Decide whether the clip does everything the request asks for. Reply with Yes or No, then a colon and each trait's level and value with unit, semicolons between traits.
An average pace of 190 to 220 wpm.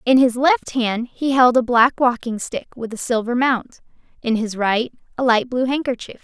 Yes: average, 200 wpm